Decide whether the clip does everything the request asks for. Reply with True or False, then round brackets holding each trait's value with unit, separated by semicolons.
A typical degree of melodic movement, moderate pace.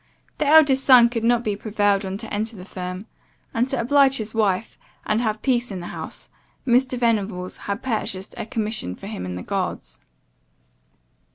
True (3.6 semitones; 180 wpm)